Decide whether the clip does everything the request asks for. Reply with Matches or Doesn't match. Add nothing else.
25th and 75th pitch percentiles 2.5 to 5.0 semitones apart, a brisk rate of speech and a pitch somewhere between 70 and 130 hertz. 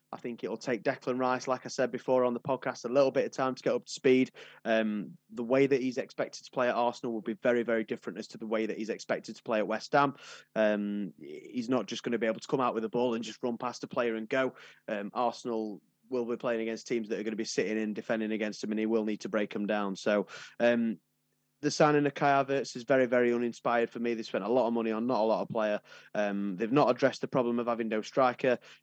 Matches